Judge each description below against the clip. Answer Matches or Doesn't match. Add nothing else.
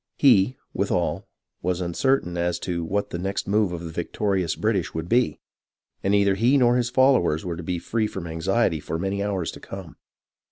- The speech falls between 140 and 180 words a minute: Doesn't match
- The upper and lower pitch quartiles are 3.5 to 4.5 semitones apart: Matches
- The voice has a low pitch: Matches